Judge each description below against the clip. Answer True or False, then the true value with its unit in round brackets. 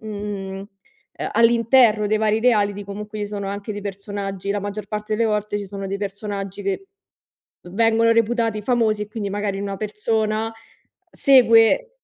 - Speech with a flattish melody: True (1.9 semitones)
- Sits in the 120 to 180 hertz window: False (210 Hz)